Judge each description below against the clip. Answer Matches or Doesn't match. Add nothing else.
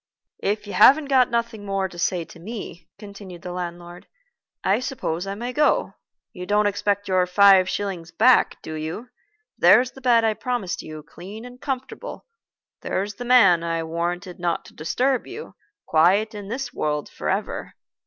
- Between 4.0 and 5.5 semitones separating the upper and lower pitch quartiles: Matches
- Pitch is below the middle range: Doesn't match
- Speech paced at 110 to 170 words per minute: Matches